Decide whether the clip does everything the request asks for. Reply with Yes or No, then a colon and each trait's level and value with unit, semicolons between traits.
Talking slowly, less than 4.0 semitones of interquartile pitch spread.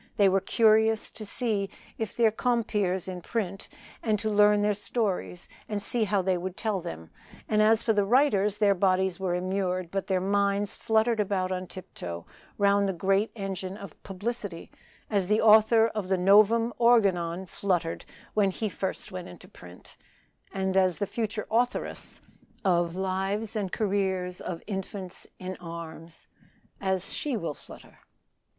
No: average, 155 wpm; narrow, 2.6 semitones